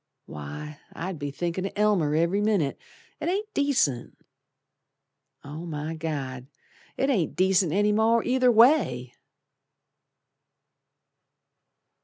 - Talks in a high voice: No, medium, 175 Hz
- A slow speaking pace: Yes, slow, 105 wpm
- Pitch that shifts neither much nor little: No, wide, 6.8 semitones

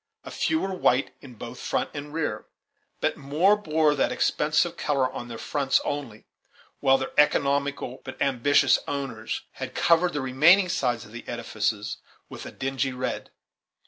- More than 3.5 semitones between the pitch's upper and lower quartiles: No, average, 3.0 semitones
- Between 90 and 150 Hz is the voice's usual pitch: Yes, low, 135 Hz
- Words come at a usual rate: Yes, average, 160 wpm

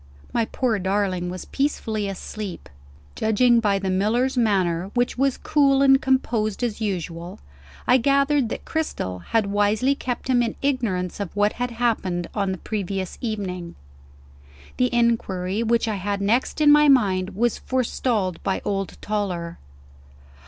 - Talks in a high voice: Yes, high, 215 Hz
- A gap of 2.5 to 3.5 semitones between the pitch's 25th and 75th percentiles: No, average, 4.5 semitones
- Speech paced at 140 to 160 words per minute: Yes, average, 150 wpm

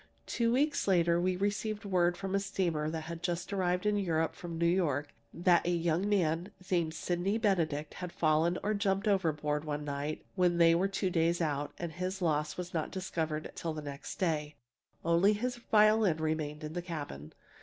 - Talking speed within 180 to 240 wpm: Yes, average, 185 wpm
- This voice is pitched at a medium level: Yes, medium, 170 Hz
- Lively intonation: No, average, 3.5 semitones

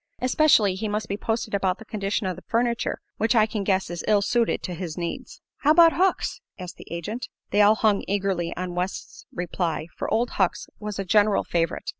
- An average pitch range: Yes, average, 3.4 semitones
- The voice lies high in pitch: Yes, high, 205 Hz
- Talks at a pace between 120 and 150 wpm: No, fast, 205 wpm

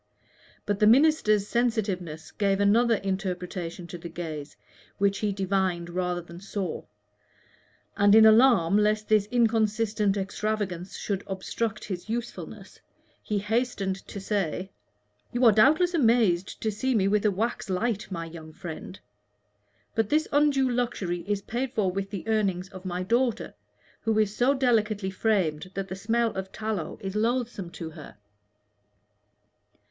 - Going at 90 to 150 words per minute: Yes, average, 145 wpm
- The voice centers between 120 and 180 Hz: No, high, 205 Hz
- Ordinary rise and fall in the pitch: Yes, average, 3.4 semitones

